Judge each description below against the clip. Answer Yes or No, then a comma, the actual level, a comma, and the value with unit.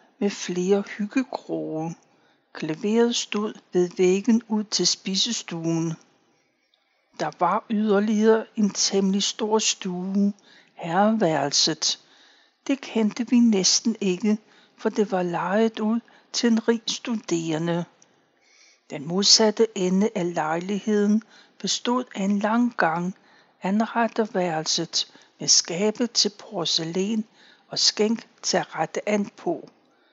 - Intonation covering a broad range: No, average, 3.5 semitones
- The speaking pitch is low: No, high, 210 Hz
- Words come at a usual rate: No, slow, 110 wpm